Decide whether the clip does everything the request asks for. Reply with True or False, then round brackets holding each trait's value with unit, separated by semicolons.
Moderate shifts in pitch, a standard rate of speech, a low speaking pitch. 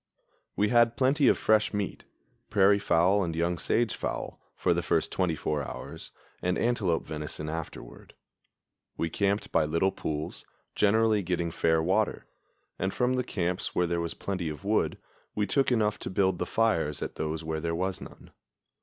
True (4.4 semitones; 170 wpm; 95 Hz)